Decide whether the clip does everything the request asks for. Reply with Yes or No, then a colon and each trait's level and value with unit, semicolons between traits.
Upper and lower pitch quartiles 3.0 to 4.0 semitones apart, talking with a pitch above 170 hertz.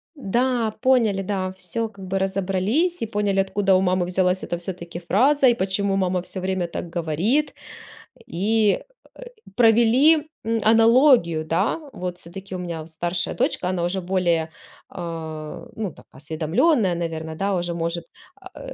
No: average, 4.4 semitones; high, 190 Hz